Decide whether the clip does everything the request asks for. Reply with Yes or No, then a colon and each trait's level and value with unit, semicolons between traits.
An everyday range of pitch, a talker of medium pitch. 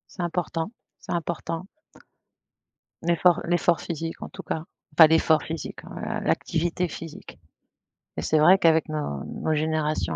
No: narrow, 1.7 semitones; medium, 160 Hz